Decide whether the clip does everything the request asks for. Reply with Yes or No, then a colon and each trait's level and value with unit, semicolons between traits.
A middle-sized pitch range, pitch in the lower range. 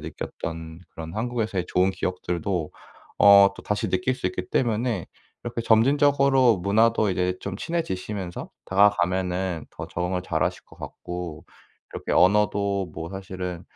Yes: average, 3.5 semitones; very low, 95 Hz